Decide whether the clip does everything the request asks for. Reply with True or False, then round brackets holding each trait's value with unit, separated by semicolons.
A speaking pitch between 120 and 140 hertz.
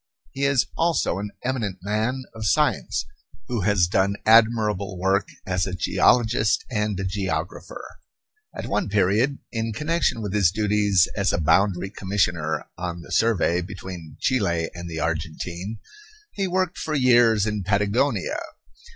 False (100 Hz)